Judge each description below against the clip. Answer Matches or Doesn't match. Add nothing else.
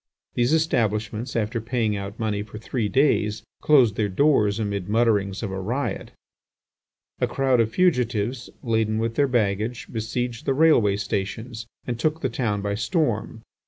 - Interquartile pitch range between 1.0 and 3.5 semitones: Matches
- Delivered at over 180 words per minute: Doesn't match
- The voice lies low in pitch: Matches